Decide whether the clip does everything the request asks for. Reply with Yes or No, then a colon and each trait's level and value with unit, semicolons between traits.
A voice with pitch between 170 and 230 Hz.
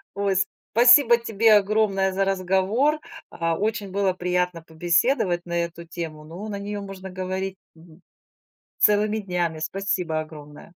Yes: high, 190 Hz